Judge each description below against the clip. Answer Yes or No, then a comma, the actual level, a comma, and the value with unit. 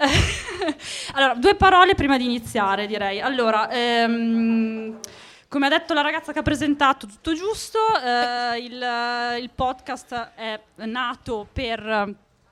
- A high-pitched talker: Yes, high, 245 Hz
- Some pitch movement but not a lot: Yes, average, 4.3 semitones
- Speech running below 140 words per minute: Yes, average, 125 wpm